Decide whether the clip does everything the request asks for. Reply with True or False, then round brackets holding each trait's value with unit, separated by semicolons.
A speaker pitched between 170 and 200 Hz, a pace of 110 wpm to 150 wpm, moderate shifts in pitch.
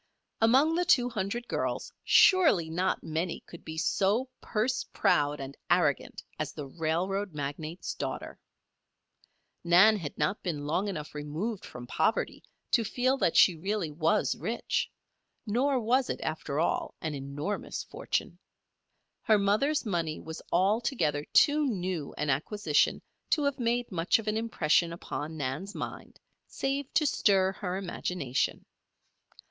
False (185 Hz; 140 wpm; 6.4 semitones)